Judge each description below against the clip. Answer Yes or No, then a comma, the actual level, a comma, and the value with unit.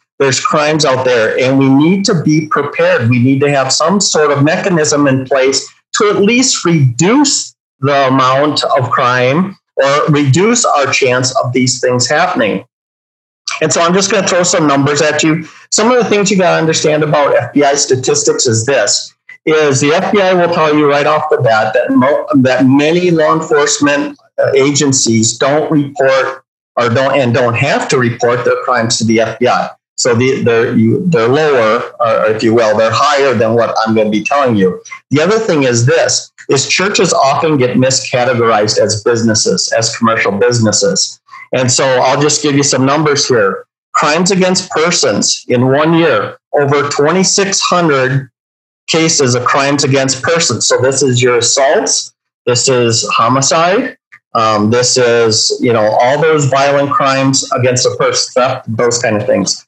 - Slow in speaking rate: No, average, 175 wpm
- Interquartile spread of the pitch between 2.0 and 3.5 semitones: No, average, 4.3 semitones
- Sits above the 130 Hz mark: Yes, medium, 140 Hz